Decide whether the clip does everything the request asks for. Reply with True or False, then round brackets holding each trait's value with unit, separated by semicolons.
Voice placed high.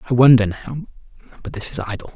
False (115 Hz)